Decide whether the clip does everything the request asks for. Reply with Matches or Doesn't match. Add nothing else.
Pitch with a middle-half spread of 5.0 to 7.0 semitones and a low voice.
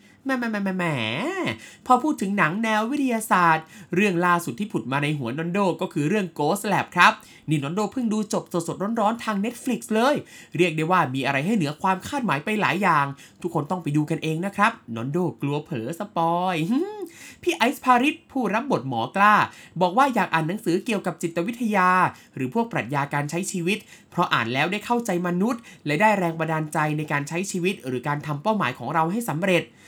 Doesn't match